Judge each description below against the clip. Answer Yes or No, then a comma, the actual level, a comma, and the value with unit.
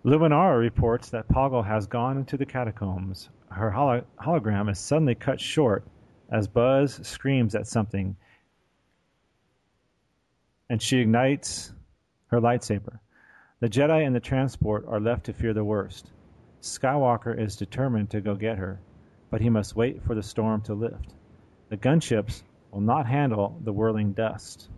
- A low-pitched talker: Yes, low, 115 Hz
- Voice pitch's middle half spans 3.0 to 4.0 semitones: Yes, average, 3.4 semitones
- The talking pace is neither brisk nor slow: Yes, average, 145 wpm